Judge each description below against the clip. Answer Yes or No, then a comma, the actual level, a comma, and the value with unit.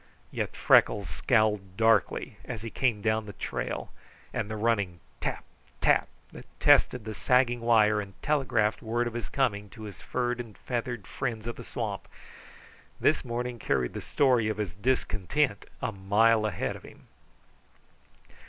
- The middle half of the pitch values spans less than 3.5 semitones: Yes, average, 2.7 semitones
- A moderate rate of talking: Yes, average, 155 wpm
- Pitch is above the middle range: No, low, 110 Hz